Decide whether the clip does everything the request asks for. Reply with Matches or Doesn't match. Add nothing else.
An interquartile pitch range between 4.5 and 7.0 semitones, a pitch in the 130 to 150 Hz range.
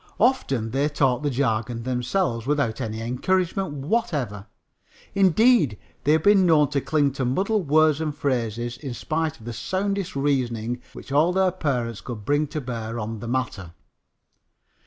Matches